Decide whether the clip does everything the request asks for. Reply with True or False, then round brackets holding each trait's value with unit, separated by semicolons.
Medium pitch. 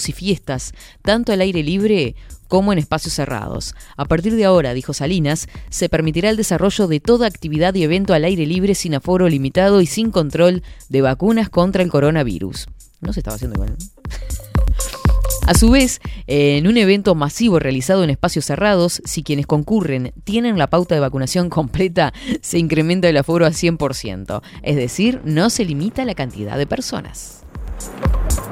True (165 Hz)